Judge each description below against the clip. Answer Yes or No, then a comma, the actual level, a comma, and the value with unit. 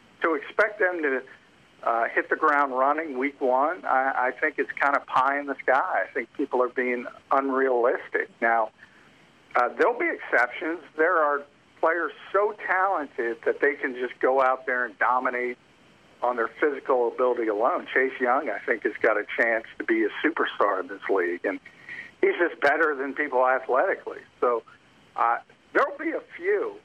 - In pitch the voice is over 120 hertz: Yes, low, 135 Hz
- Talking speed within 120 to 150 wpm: No, average, 175 wpm